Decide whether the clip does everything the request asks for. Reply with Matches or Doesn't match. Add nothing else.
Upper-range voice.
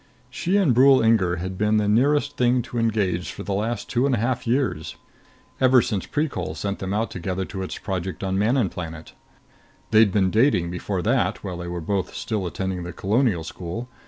Doesn't match